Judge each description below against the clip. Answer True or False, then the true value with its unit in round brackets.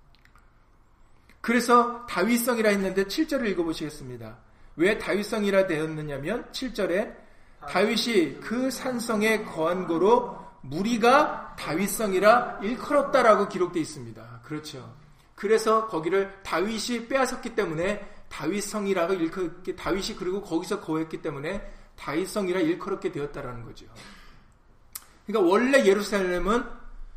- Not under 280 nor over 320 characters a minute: True (305 characters per minute)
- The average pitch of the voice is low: False (200 Hz)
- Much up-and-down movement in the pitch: True (6.4 semitones)